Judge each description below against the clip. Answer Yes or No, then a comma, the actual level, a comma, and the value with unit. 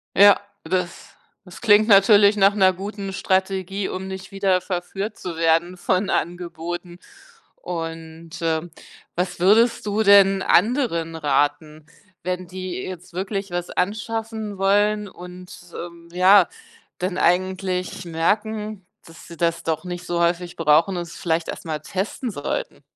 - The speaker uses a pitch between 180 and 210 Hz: Yes, medium, 185 Hz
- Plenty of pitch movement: No, narrow, 2.6 semitones